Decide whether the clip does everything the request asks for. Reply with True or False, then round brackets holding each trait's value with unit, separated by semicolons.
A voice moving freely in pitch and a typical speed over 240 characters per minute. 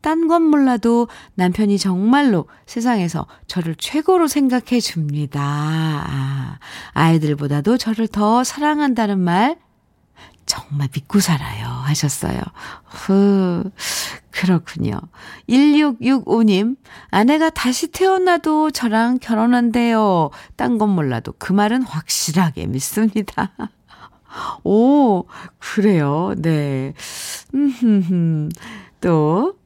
False (7.9 semitones; 200 characters per minute)